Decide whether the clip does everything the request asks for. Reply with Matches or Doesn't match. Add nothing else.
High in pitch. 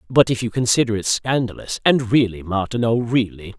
Doesn't match